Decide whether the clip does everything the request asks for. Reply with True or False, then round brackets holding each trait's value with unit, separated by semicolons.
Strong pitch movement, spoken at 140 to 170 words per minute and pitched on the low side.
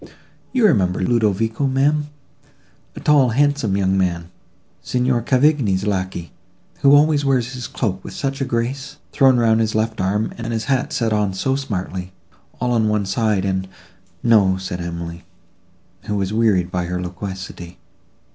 True (5.8 semitones; 145 wpm; 110 Hz)